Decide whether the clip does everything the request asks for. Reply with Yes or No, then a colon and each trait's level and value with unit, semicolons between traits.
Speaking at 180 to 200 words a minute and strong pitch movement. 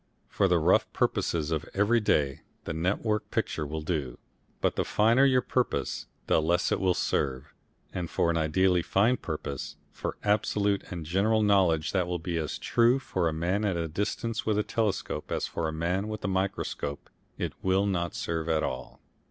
No: average, 190 wpm; average, 4.6 semitones